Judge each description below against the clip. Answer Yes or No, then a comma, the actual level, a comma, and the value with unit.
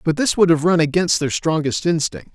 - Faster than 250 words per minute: No, fast, 230 wpm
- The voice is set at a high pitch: No, medium, 165 Hz